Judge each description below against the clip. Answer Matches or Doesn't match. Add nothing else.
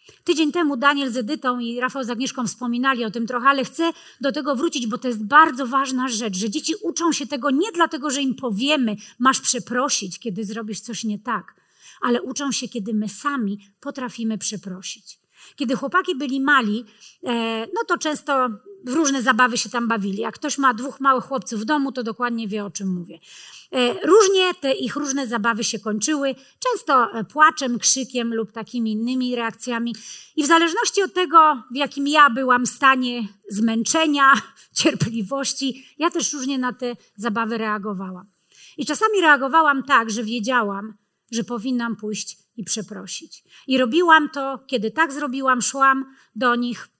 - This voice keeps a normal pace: Doesn't match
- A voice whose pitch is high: Matches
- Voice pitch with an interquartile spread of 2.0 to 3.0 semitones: Doesn't match